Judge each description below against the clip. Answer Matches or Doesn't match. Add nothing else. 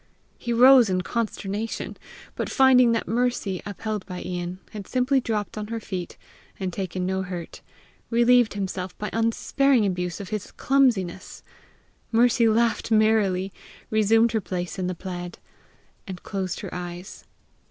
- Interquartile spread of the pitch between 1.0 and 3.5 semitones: Doesn't match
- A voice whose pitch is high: Matches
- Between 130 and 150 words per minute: Matches